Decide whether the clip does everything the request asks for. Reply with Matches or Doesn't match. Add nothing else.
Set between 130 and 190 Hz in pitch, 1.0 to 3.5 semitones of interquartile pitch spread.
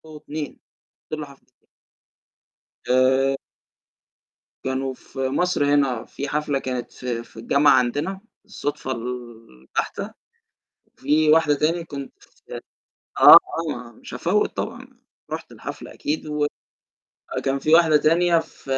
Matches